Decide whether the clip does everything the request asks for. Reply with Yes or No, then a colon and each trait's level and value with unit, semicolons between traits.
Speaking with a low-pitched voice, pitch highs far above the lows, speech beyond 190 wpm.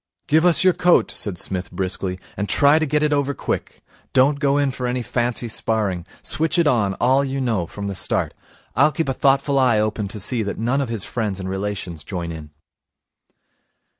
Yes: low, 120 Hz; wide, 6.0 semitones; average, 200 wpm